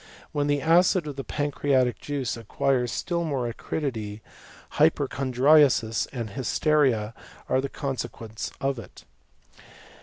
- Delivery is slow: Yes, slow, 115 wpm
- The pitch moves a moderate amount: Yes, average, 3.6 semitones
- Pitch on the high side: No, low, 135 Hz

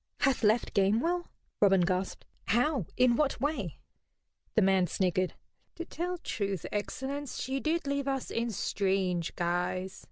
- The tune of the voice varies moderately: No, wide, 6.8 semitones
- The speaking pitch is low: No, high, 215 Hz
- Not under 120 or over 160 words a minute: Yes, slow, 135 wpm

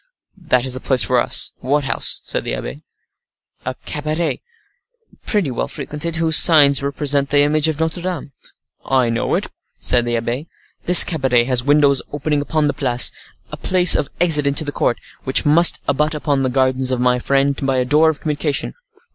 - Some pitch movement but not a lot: Yes, average, 3.1 semitones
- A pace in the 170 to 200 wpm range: Yes, average, 185 wpm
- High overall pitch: No, medium, 145 Hz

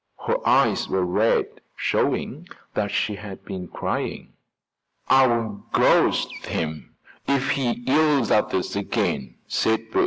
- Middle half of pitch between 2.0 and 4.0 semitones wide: No, average, 5.3 semitones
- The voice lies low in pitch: Yes, low, 105 Hz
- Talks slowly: Yes, slow, 125 wpm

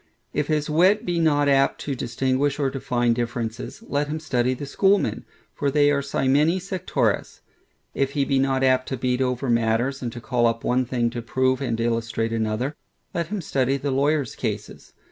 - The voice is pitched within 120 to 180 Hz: Yes, low, 135 Hz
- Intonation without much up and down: No, average, 3.2 semitones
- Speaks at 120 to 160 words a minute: No, average, 185 wpm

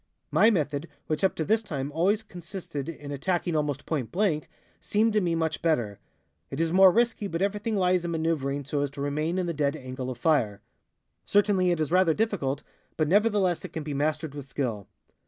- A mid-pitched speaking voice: Yes, medium, 160 Hz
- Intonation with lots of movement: No, average, 4.7 semitones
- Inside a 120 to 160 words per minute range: No, average, 200 wpm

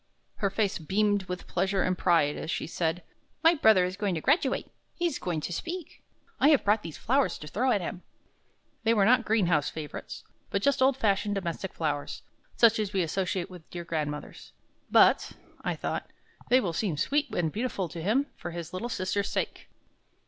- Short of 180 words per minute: No, average, 190 wpm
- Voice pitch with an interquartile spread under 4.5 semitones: No, average, 4.8 semitones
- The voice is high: Yes, high, 195 Hz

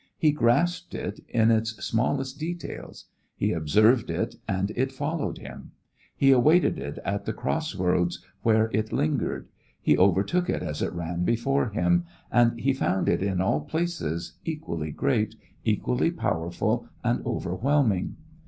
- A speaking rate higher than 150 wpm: No, average, 145 wpm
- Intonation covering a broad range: Yes, wide, 7.5 semitones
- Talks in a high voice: No, low, 110 Hz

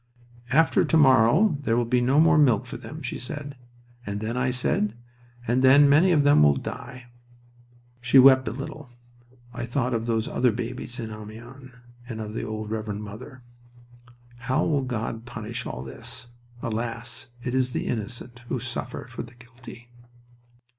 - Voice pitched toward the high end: No, low, 120 Hz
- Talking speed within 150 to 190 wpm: Yes, average, 165 wpm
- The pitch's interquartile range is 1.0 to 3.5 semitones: Yes, narrow, 2.5 semitones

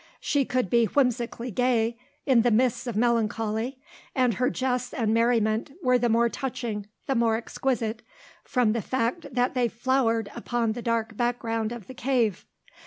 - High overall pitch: Yes, high, 235 Hz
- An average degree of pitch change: No, narrow, 1.9 semitones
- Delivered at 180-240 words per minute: No, average, 165 wpm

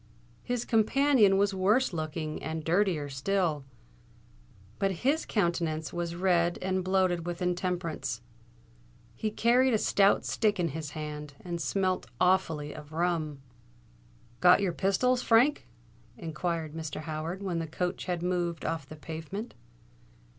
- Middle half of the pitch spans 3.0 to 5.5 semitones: Yes, average, 3.7 semitones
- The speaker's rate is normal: No, slow, 130 wpm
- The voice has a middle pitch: Yes, medium, 175 Hz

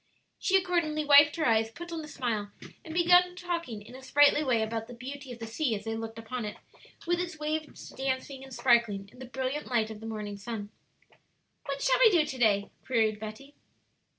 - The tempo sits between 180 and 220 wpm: Yes, fast, 205 wpm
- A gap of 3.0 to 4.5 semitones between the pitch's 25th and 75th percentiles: No, wide, 5.5 semitones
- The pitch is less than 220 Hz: No, very high, 260 Hz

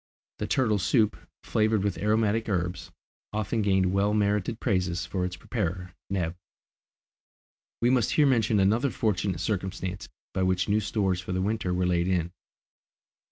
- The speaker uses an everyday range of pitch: Yes, average, 3.0 semitones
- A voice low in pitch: Yes, low, 100 Hz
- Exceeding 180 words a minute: No, average, 150 wpm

